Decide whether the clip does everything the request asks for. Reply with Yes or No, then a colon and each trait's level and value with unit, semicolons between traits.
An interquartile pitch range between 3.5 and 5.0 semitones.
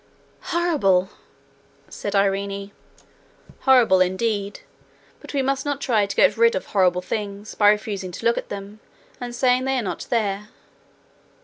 Yes: average, 4.2 semitones